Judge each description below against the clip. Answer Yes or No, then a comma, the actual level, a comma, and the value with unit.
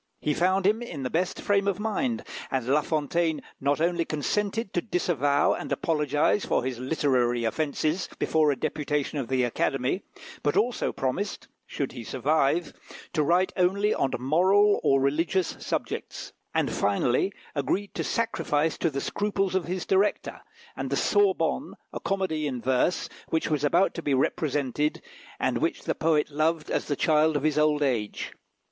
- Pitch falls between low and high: Yes, medium, 155 Hz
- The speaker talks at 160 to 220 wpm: Yes, average, 165 wpm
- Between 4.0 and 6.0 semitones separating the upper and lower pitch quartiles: Yes, average, 5.0 semitones